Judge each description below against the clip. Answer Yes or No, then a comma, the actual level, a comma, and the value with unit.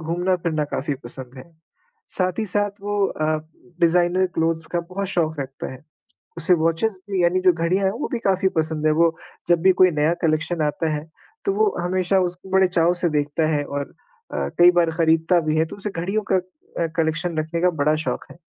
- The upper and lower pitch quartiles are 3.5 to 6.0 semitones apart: No, average, 2.7 semitones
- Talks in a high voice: No, medium, 170 Hz